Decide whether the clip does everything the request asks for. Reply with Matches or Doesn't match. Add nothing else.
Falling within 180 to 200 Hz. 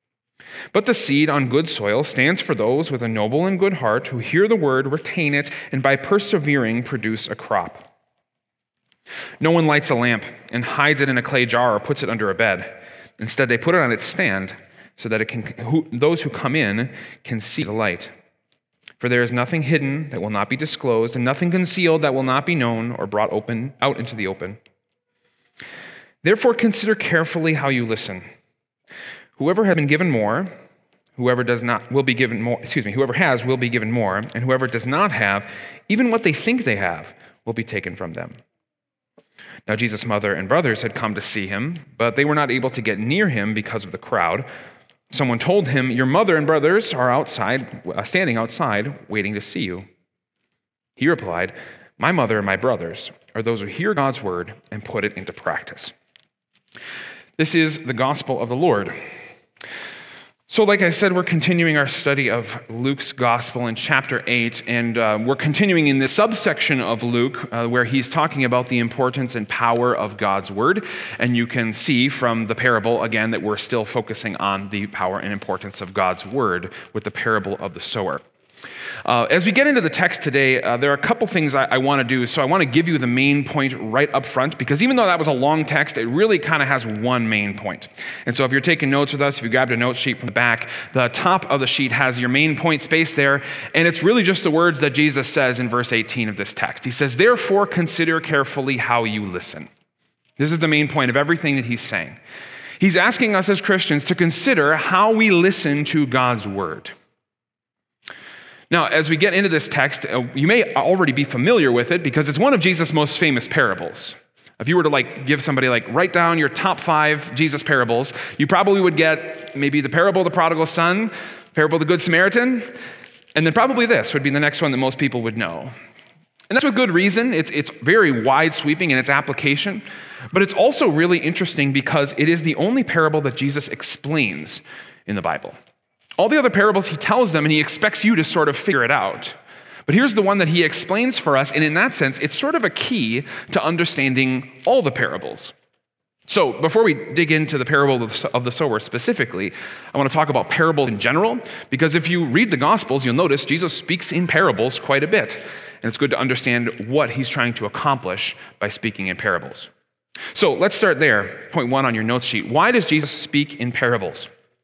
Doesn't match